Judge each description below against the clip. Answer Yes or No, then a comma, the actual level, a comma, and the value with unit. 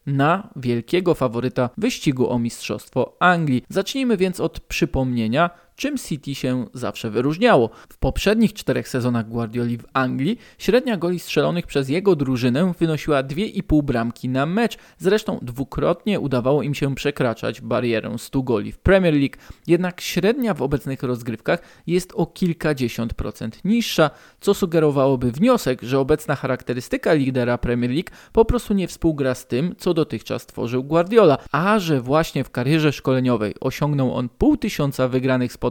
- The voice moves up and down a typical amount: No, wide, 6.2 semitones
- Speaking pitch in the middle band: Yes, medium, 145 Hz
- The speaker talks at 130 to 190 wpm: Yes, average, 145 wpm